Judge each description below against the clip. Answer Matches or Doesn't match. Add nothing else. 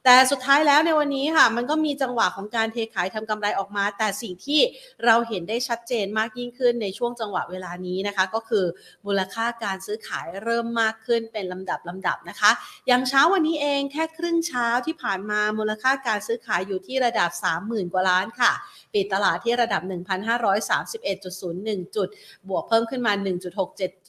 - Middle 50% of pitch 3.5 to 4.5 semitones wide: Matches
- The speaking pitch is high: Matches